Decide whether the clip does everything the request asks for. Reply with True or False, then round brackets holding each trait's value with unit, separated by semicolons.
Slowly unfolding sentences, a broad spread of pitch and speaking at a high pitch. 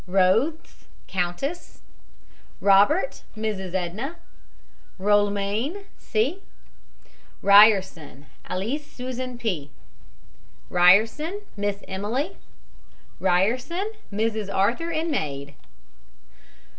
True (70 wpm; 6.3 semitones; 210 Hz)